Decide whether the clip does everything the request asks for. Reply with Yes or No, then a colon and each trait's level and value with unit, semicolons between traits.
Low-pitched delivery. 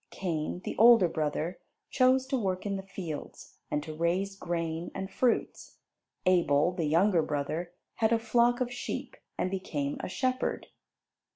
No: medium, 185 Hz